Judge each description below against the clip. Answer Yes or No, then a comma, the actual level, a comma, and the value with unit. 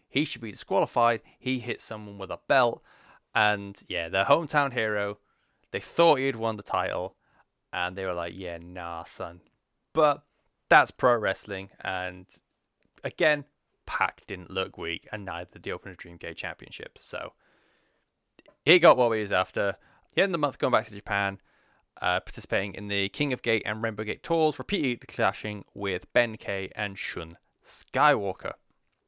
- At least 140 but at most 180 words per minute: Yes, average, 170 wpm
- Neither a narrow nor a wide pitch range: Yes, average, 3.8 semitones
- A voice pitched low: Yes, low, 105 Hz